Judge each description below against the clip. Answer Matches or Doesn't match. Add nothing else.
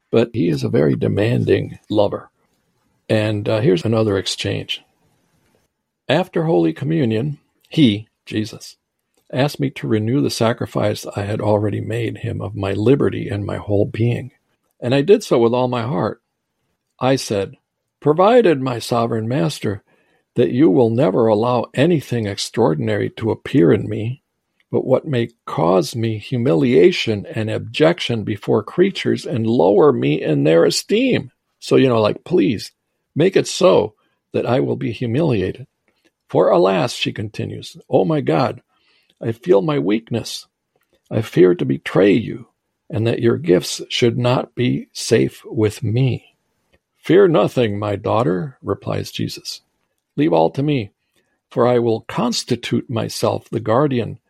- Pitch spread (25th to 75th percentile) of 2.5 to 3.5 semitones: Doesn't match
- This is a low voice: Matches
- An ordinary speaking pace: Matches